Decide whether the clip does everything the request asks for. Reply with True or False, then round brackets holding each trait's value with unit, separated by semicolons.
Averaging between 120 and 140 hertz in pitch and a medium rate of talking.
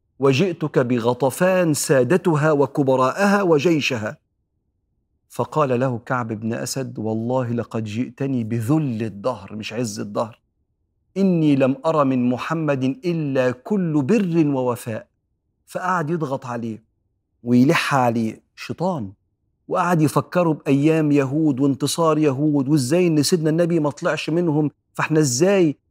True (135 Hz; 110 wpm)